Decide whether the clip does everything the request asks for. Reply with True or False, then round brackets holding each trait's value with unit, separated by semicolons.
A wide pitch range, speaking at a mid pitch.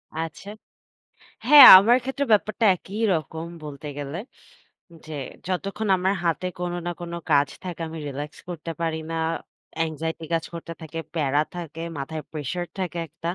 False (2.7 semitones; 165 Hz)